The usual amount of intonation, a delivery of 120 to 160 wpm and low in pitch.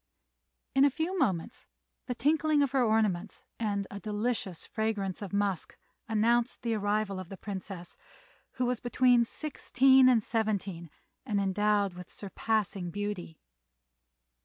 No: average, 3.8 semitones; slow, 135 wpm; high, 215 Hz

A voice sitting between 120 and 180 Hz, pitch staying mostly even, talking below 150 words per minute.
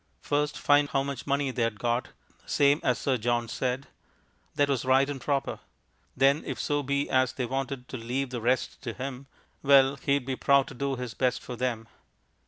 No: low, 135 Hz; narrow, 1.9 semitones; average, 190 wpm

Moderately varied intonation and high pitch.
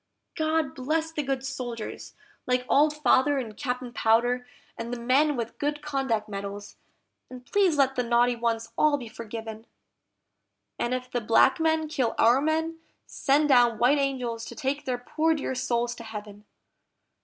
Yes: average, 3.8 semitones; very high, 255 Hz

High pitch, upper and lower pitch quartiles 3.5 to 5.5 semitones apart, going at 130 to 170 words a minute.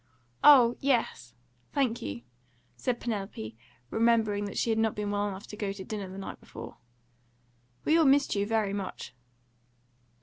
No: high, 210 Hz; average, 3.1 semitones; average, 160 wpm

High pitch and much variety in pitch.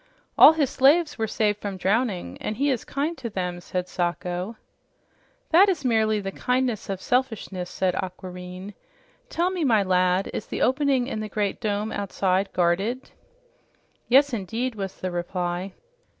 Yes: high, 210 Hz; wide, 5.7 semitones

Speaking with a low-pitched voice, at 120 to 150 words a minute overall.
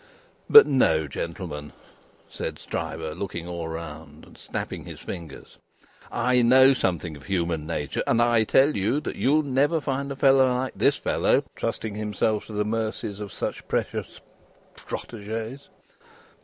Yes: low, 105 Hz; average, 145 wpm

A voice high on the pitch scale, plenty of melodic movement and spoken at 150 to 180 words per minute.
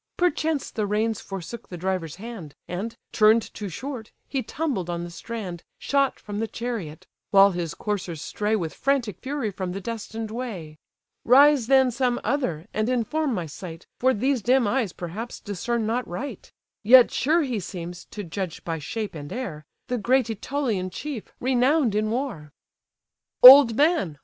Yes: high, 220 Hz; wide, 5.8 semitones; average, 165 wpm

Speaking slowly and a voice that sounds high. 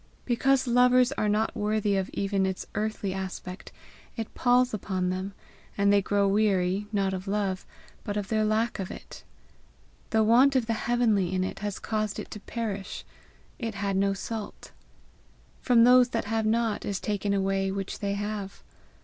No: average, 175 wpm; high, 205 Hz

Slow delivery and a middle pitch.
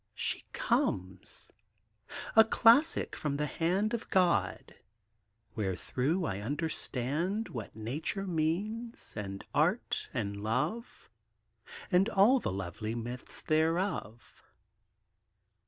Yes: slow, 95 wpm; medium, 155 Hz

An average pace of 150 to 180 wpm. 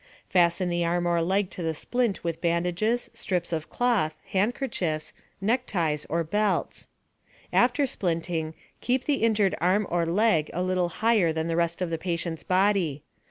Yes: average, 160 wpm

